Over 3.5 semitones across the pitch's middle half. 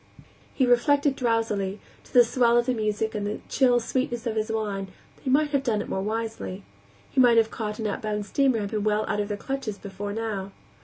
No: average, 2.8 semitones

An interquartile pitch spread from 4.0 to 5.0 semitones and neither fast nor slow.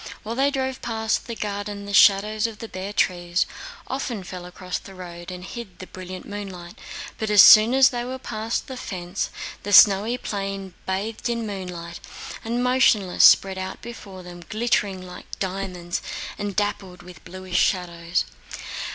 No: average, 3.4 semitones; average, 160 wpm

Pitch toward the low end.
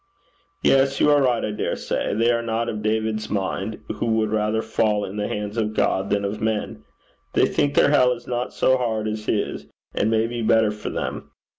Yes: low, 110 Hz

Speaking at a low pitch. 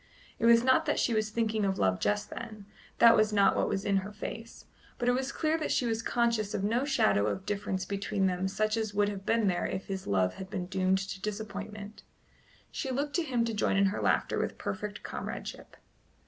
No: high, 210 Hz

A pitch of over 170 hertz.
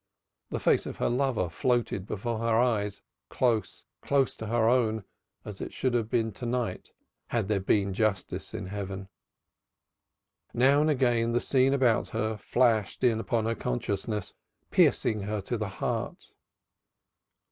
No: low, 110 Hz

